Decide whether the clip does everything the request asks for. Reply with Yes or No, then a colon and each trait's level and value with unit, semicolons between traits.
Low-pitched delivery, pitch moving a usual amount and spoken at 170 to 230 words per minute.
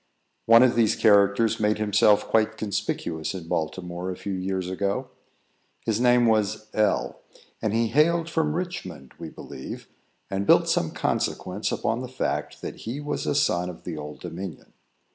No: low, 105 Hz; average, 4.2 semitones; average, 160 wpm